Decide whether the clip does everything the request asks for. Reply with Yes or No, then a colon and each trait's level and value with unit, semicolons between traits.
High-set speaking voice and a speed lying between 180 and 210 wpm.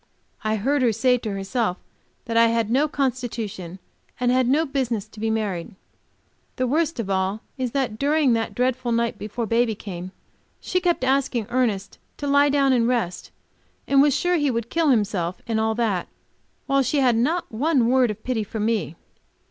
Yes: high, 235 Hz; average, 185 wpm